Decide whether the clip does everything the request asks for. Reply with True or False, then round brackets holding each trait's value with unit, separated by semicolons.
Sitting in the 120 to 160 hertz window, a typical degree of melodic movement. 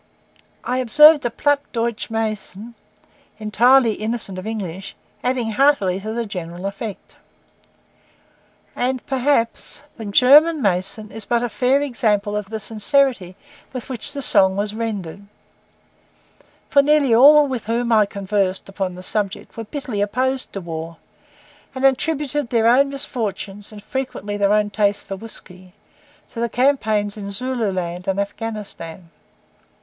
False (220 Hz; 4.2 semitones)